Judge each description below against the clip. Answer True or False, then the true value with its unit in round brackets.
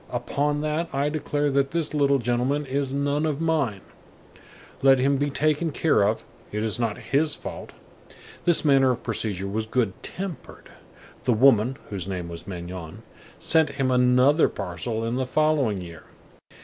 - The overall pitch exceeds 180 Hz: False (135 Hz)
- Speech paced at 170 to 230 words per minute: False (160 wpm)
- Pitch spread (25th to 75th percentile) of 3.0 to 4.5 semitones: False (5.0 semitones)